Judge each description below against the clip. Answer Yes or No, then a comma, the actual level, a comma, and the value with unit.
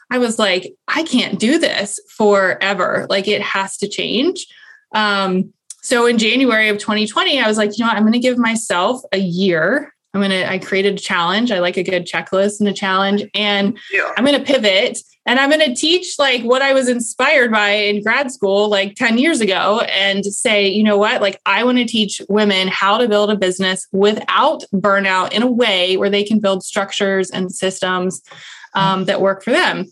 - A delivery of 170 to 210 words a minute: Yes, fast, 205 wpm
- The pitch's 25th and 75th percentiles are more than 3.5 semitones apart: Yes, average, 4.1 semitones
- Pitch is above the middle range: Yes, high, 205 Hz